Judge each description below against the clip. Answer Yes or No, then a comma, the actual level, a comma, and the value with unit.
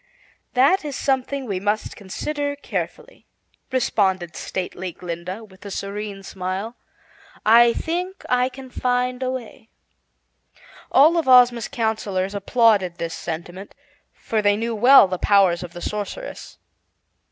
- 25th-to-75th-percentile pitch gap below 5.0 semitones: No, average, 5.3 semitones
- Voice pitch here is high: Yes, high, 220 Hz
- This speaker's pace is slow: Yes, slow, 130 wpm